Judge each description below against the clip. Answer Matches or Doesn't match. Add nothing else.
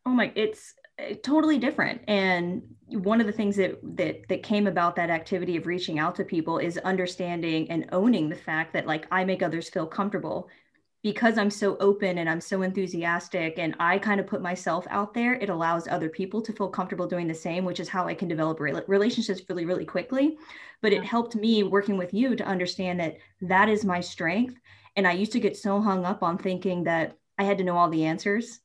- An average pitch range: Matches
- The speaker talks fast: Matches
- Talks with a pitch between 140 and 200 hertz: Matches